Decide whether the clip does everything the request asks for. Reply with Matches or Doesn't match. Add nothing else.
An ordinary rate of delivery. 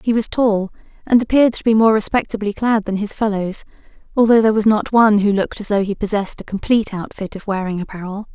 Doesn't match